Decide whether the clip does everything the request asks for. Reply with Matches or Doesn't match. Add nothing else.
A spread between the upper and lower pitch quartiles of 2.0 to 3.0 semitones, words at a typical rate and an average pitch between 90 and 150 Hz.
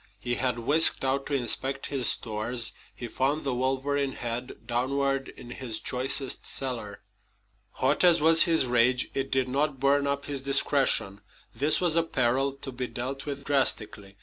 Matches